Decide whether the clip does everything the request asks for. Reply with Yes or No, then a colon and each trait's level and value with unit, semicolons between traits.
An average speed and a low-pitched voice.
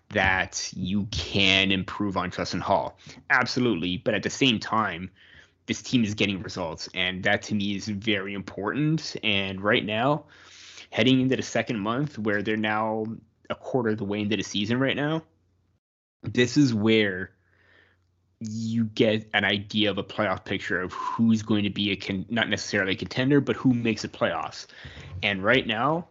Yes: average, 175 wpm; low, 105 Hz